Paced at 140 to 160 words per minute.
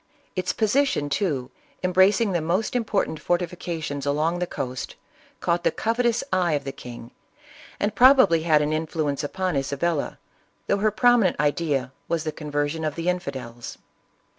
Yes: average, 150 wpm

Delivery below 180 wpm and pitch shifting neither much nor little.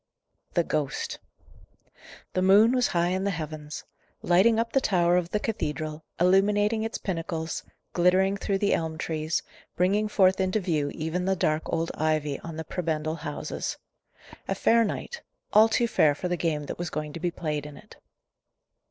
Yes: average, 170 wpm; average, 4.1 semitones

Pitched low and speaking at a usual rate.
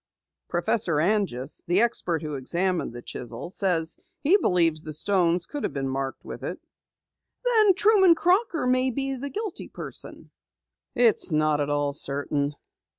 No: medium, 175 Hz; average, 150 wpm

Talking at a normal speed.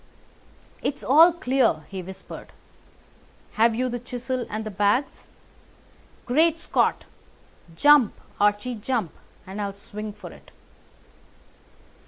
No: slow, 110 wpm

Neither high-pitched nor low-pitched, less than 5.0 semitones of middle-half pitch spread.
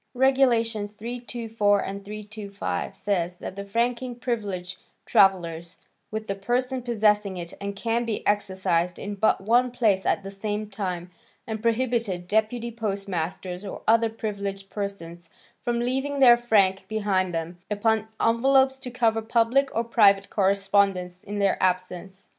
No: high, 205 Hz; average, 3.3 semitones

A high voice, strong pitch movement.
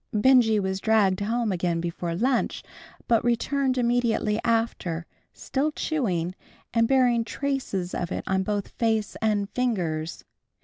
No: high, 220 Hz; average, 4.3 semitones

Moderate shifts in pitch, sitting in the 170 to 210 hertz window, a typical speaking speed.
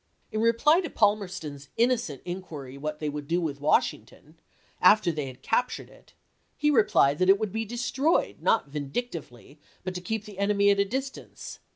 No: wide, 6.9 semitones; high, 190 Hz; average, 180 wpm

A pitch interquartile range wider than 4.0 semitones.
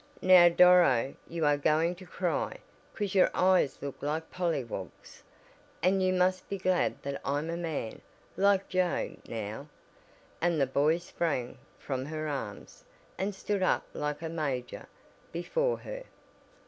Yes: average, 4.6 semitones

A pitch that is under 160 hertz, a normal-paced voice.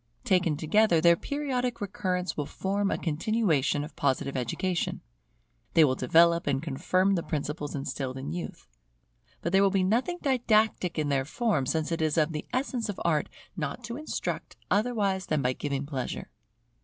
No: medium, 170 Hz; average, 170 wpm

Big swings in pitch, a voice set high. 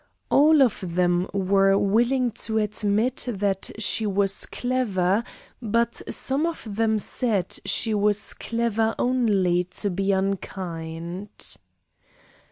No: average, 3.4 semitones; high, 205 Hz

